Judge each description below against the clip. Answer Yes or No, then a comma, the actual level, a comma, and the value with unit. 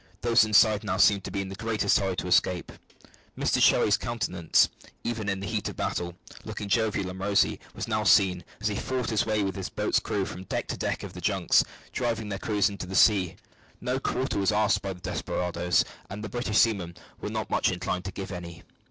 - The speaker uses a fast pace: Yes, fast, 215 wpm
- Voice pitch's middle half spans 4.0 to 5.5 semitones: No, narrow, 2.5 semitones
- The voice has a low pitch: Yes, low, 100 Hz